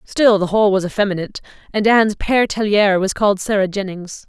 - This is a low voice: No, high, 200 Hz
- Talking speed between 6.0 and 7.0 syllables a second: Yes, 6.3 syllables/s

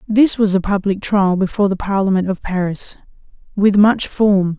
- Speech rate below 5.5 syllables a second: Yes, 4.9 syllables/s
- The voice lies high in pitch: Yes, high, 195 Hz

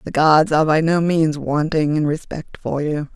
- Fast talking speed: Yes, fast, 210 wpm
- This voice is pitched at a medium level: Yes, medium, 155 Hz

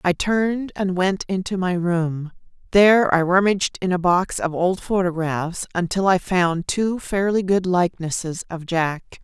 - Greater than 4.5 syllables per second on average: No, 4.4 syllables/s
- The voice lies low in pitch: No, medium, 180 Hz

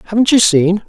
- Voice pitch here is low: No, high, 200 Hz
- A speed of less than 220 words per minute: Yes, fast, 205 wpm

